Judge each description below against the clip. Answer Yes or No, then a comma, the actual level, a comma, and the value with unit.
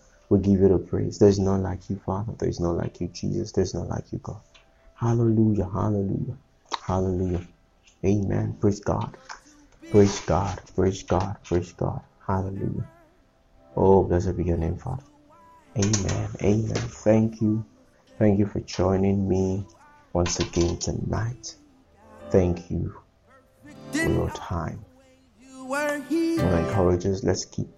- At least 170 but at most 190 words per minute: No, slow, 135 wpm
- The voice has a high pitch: No, low, 100 Hz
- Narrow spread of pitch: No, average, 4.2 semitones